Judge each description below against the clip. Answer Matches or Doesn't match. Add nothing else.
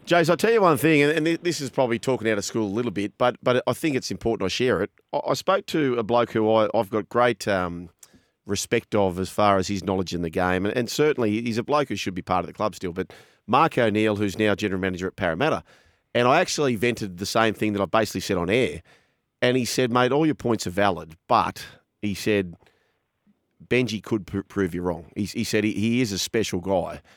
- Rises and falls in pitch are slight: Doesn't match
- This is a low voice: Matches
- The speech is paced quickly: Matches